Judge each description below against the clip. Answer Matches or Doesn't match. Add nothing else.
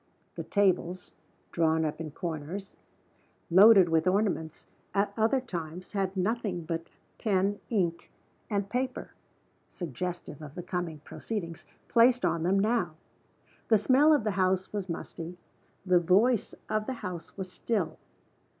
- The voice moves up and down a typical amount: Matches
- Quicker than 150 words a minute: Doesn't match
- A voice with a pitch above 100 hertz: Matches